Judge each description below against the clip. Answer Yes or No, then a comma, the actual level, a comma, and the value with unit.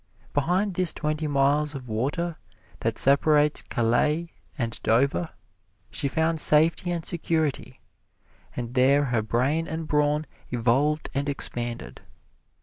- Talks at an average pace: No, slow, 120 wpm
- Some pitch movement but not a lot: Yes, average, 4.0 semitones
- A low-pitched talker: No, medium, 145 Hz